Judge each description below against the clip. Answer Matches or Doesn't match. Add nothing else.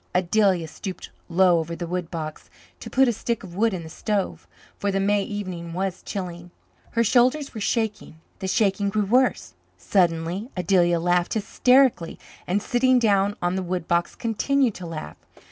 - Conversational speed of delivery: Matches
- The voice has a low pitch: Doesn't match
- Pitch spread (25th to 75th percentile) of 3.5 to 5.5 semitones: Matches